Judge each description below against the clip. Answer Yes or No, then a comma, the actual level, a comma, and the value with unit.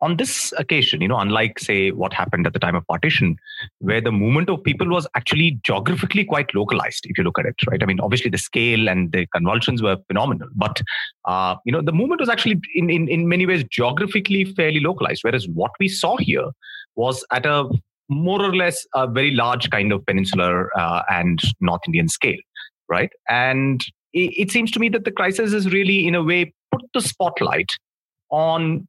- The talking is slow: No, average, 200 wpm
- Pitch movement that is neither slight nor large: No, wide, 7.6 semitones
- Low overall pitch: No, medium, 160 Hz